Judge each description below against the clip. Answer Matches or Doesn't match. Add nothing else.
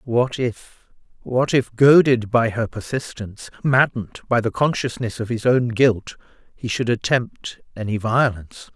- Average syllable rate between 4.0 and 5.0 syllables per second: Matches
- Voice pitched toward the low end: Matches